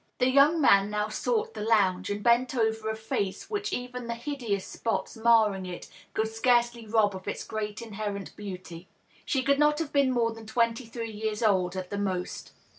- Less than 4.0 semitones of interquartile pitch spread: Yes, average, 3.2 semitones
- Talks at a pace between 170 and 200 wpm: Yes, average, 190 wpm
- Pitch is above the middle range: Yes, high, 220 Hz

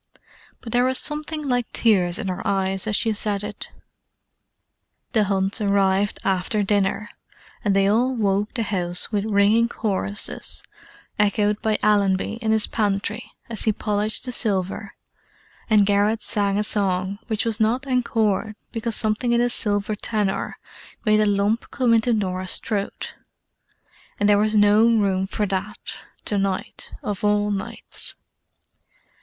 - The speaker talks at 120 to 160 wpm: Yes, average, 145 wpm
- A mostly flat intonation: Yes, narrow, 1.9 semitones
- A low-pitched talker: No, high, 210 Hz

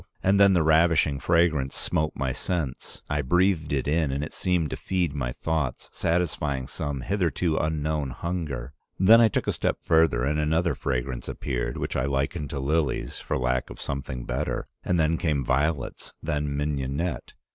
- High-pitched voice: No, very low, 75 Hz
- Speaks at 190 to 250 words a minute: No, average, 170 wpm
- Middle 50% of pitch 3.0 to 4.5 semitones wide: Yes, average, 3.5 semitones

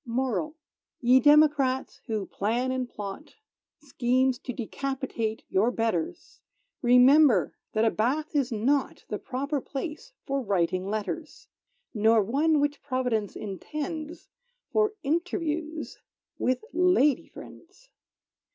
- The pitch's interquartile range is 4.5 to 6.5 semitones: Yes, average, 4.9 semitones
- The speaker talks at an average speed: No, slow, 110 wpm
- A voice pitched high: Yes, very high, 260 Hz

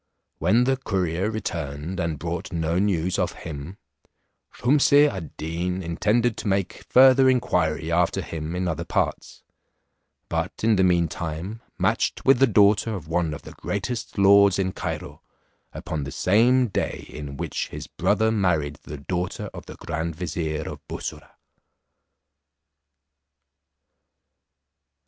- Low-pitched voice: Yes, very low, 90 Hz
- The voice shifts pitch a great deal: No, average, 4.8 semitones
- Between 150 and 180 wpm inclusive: No, slow, 135 wpm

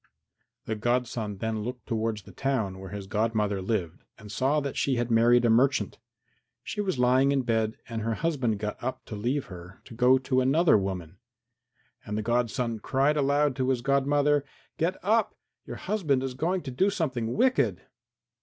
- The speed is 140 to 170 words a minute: No, average, 180 wpm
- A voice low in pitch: Yes, low, 125 Hz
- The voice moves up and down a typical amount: Yes, average, 4.1 semitones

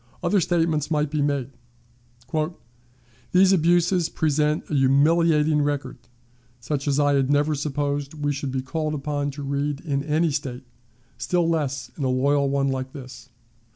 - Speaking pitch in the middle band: Yes, medium, 145 Hz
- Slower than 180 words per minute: Yes, average, 155 wpm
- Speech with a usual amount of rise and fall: No, narrow, 2.1 semitones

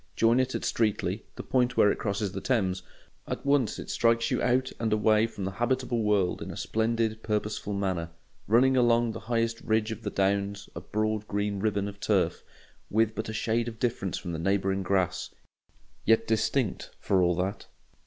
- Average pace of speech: Yes, average, 190 wpm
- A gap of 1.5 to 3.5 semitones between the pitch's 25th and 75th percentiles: Yes, narrow, 2.6 semitones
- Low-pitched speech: Yes, low, 110 Hz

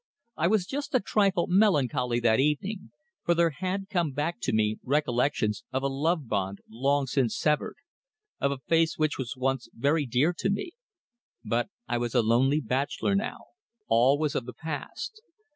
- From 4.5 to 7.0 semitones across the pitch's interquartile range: Yes, wide, 5.6 semitones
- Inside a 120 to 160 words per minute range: No, average, 175 wpm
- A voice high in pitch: No, medium, 140 Hz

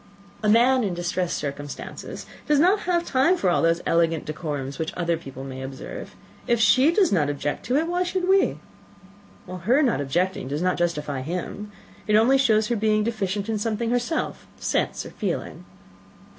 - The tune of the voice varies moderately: No, wide, 7.6 semitones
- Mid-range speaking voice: No, high, 205 Hz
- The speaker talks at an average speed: Yes, average, 170 wpm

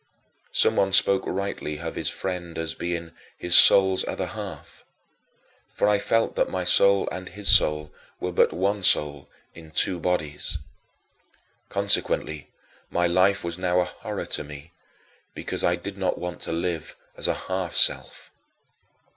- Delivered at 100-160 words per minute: Yes, average, 150 wpm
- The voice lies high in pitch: No, very low, 90 Hz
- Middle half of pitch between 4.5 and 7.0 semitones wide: No, narrow, 2.6 semitones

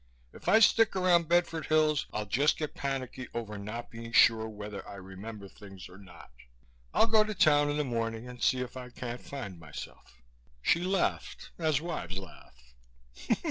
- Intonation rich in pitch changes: Yes, wide, 7.1 semitones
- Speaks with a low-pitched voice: Yes, low, 125 Hz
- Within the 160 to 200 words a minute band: Yes, average, 175 wpm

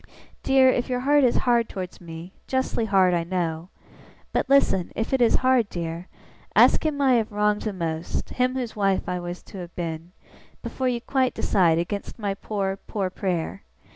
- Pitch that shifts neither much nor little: No, wide, 6.0 semitones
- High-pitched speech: Yes, high, 200 Hz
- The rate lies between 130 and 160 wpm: No, average, 185 wpm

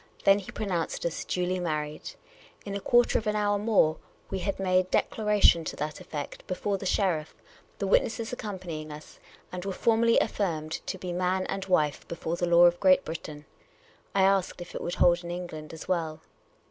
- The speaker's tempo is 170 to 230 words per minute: Yes, average, 185 wpm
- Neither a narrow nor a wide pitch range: Yes, average, 3.2 semitones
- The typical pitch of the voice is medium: Yes, medium, 180 Hz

